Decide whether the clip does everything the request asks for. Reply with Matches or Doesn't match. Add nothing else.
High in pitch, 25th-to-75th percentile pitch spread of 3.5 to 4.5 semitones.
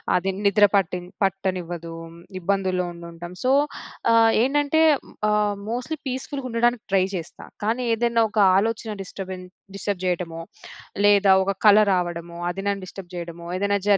Matches